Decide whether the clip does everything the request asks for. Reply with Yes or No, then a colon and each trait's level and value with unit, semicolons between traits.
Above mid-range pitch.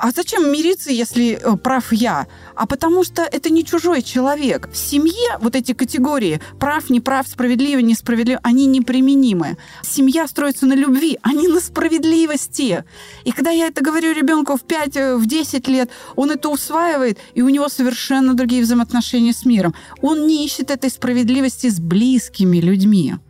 Yes: very high, 265 Hz